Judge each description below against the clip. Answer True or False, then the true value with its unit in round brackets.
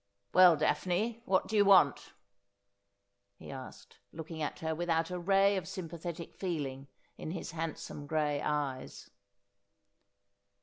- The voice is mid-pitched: True (160 Hz)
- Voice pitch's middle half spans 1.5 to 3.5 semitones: False (4.1 semitones)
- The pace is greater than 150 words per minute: False (135 wpm)